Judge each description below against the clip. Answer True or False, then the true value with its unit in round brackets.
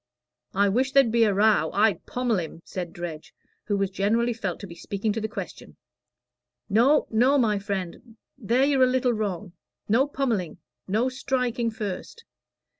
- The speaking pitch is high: True (220 Hz)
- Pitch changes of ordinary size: True (4.2 semitones)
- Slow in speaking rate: False (165 wpm)